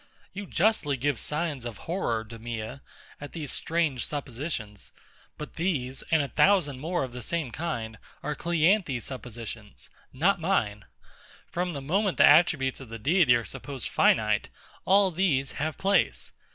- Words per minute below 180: Yes, average, 150 wpm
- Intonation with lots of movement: Yes, wide, 5.9 semitones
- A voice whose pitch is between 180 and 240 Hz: No, medium, 145 Hz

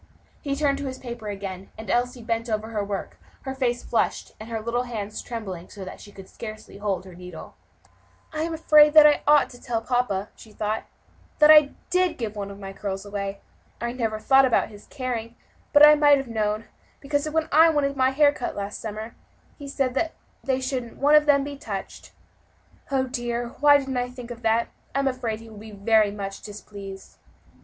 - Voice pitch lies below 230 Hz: No, high, 235 Hz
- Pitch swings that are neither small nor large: Yes, average, 4.9 semitones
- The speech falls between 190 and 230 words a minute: Yes, average, 200 wpm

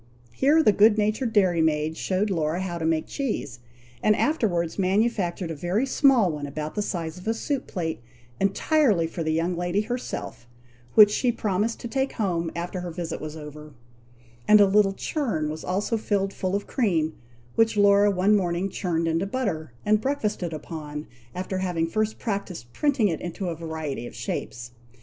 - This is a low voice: No, medium, 185 Hz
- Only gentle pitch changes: No, average, 4.6 semitones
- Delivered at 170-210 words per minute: Yes, average, 175 wpm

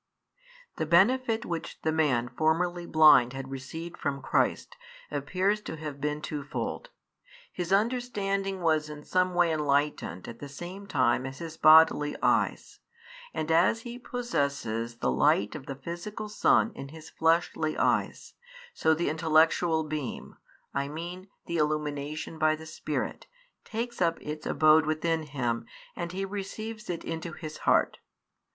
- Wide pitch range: No, average, 3.4 semitones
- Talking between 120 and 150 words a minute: Yes, average, 145 wpm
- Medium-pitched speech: Yes, medium, 160 Hz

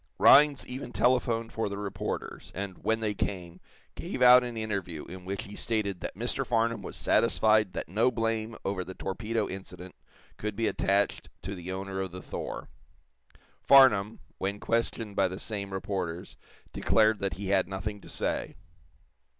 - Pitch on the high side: No, low, 100 Hz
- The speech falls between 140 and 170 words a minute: Yes, average, 165 wpm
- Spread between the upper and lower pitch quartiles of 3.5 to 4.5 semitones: No, average, 3.0 semitones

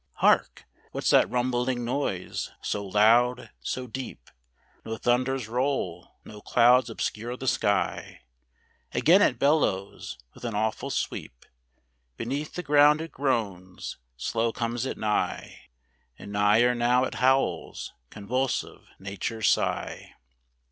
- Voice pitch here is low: Yes, low, 120 Hz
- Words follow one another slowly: Yes, slow, 120 wpm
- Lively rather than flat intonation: No, average, 3.8 semitones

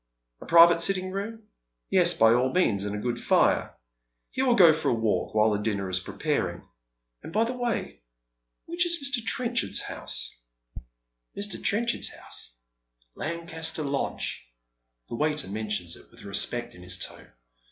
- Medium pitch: Yes, medium, 160 Hz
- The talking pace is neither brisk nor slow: Yes, average, 155 wpm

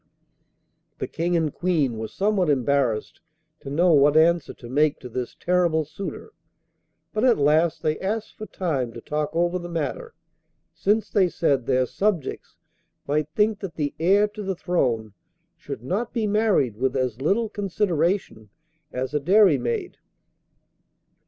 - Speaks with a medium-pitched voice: Yes, medium, 165 Hz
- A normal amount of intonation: No, wide, 6.1 semitones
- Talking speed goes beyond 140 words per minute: Yes, average, 150 wpm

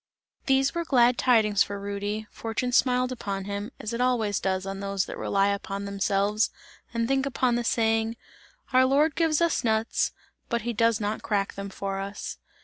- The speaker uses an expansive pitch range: No, average, 3.9 semitones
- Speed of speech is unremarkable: Yes, average, 180 wpm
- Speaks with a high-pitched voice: Yes, high, 220 Hz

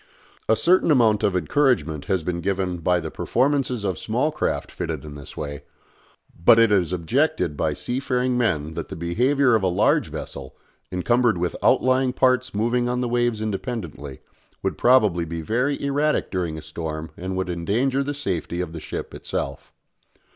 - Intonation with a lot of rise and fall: Yes, wide, 6.8 semitones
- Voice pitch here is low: Yes, low, 105 Hz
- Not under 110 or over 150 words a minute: No, average, 175 wpm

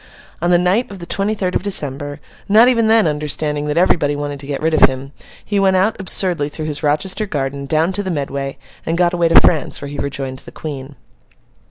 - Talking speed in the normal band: No, fast, 220 wpm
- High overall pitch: No, medium, 155 Hz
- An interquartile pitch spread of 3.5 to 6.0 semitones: Yes, average, 4.6 semitones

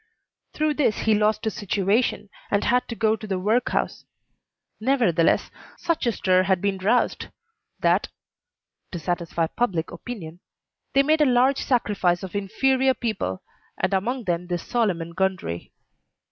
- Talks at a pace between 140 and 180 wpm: Yes, average, 145 wpm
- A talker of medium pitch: No, high, 210 Hz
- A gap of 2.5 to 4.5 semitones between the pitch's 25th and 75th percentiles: No, average, 5.0 semitones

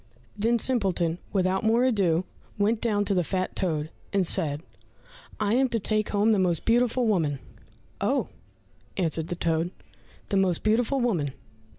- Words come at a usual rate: Yes, average, 155 wpm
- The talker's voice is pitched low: No, high, 195 Hz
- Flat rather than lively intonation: No, average, 4.6 semitones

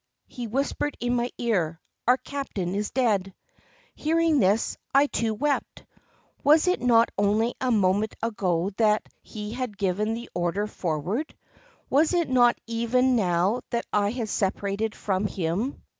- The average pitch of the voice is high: Yes, high, 225 Hz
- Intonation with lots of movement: No, average, 4.1 semitones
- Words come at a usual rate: Yes, average, 145 wpm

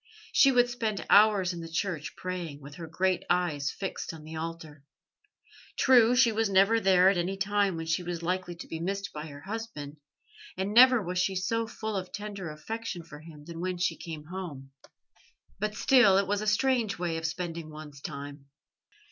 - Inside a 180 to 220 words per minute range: Yes, average, 190 wpm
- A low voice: No, medium, 180 Hz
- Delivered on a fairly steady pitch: No, average, 4.2 semitones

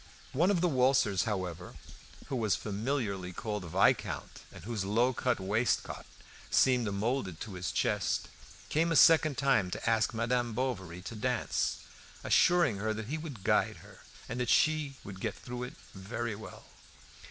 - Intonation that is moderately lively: Yes, average, 4.7 semitones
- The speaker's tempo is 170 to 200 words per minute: No, average, 160 wpm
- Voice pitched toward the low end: Yes, low, 115 Hz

